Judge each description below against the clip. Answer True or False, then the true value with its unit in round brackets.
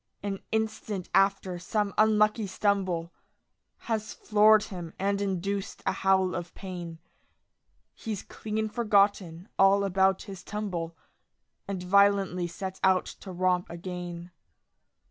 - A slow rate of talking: True (115 wpm)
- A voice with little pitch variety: True (2.3 semitones)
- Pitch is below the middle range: False (195 Hz)